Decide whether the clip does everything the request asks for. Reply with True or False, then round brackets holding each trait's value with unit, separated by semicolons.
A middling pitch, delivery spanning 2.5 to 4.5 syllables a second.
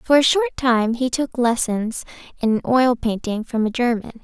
False (240 Hz; 4.4 syllables/s)